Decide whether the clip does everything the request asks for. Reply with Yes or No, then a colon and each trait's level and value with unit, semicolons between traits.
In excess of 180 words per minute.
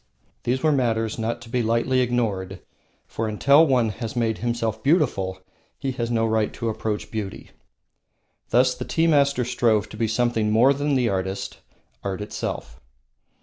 No: average, 160 wpm